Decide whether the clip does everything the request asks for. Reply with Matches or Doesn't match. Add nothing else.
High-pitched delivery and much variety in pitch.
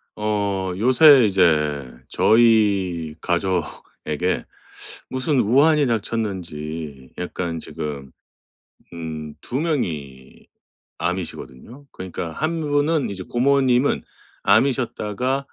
Doesn't match